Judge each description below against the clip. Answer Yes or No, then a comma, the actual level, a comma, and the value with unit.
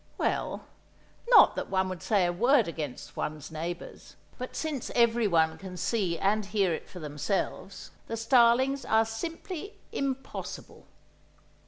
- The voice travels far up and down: Yes, wide, 5.9 semitones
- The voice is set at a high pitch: Yes, high, 210 Hz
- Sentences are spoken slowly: Yes, slow, 130 wpm